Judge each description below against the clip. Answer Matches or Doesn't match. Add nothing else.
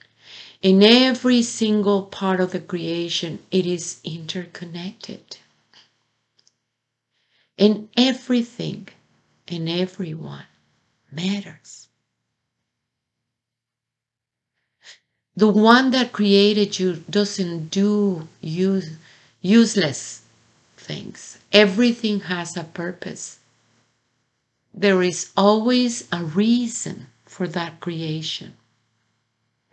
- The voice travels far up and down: Matches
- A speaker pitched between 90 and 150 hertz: Doesn't match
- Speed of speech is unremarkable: Doesn't match